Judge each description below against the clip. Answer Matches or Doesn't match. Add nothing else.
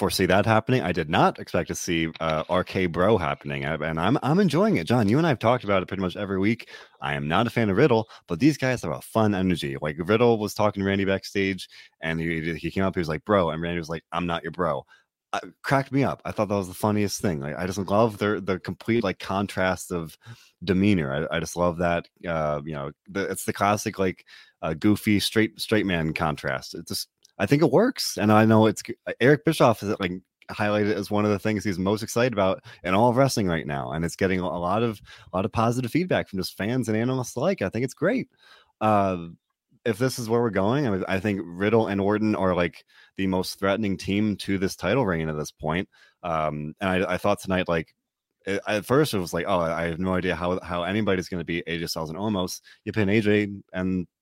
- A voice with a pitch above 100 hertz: Doesn't match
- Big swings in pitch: Doesn't match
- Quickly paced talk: Matches